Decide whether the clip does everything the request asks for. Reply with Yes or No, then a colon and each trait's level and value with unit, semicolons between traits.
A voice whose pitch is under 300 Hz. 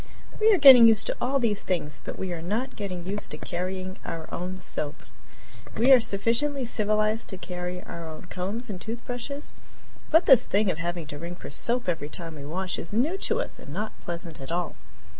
Yes: high, 190 Hz